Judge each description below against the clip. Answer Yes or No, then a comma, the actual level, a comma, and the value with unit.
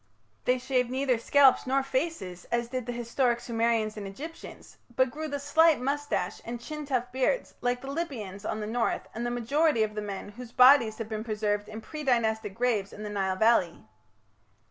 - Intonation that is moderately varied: Yes, average, 3.8 semitones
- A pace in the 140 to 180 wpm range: No, average, 190 wpm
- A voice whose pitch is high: Yes, high, 240 Hz